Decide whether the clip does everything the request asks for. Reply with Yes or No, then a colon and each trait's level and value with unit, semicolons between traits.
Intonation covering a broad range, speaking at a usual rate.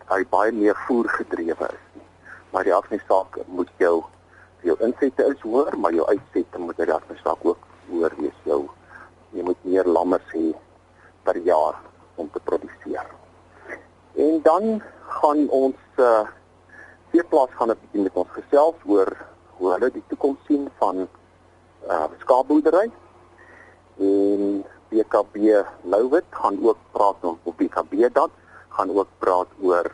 Yes: wide, 8.2 semitones; average, 150 wpm